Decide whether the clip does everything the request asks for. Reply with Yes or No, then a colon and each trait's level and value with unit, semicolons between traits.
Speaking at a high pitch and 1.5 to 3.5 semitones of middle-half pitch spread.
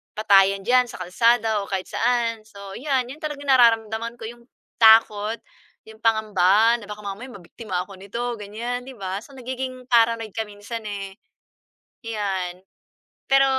Yes: high, 225 Hz; average, 3.1 semitones